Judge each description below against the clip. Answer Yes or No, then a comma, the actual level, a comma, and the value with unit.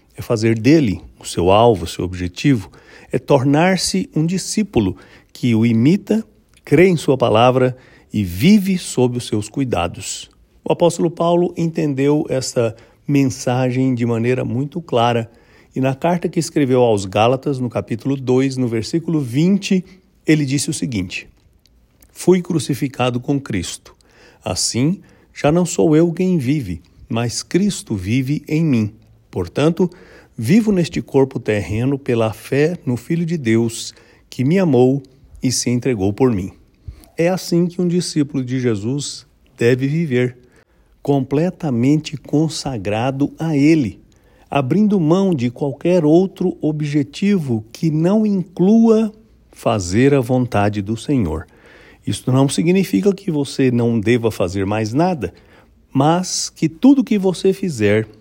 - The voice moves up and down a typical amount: No, wide, 6.2 semitones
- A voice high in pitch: No, low, 135 Hz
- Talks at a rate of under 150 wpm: Yes, slow, 135 wpm